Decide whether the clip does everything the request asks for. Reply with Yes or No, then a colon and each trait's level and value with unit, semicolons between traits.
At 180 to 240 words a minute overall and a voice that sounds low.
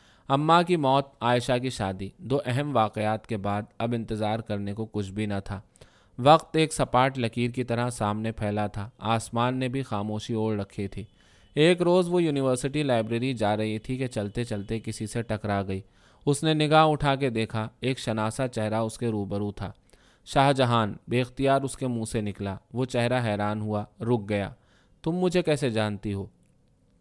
Yes: average, 185 wpm; low, 115 Hz